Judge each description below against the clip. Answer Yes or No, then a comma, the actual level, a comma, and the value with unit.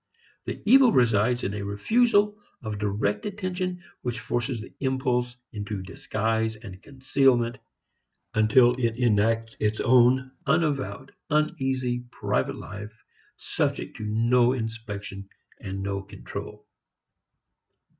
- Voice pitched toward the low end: Yes, low, 120 Hz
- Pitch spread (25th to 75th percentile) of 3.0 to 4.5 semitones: Yes, average, 4.0 semitones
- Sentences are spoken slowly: Yes, slow, 110 wpm